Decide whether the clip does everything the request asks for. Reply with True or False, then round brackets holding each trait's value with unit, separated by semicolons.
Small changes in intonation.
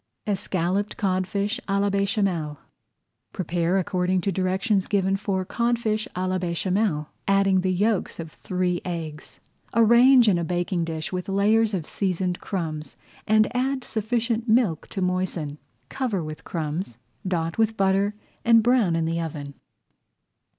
False (3.7 semitones)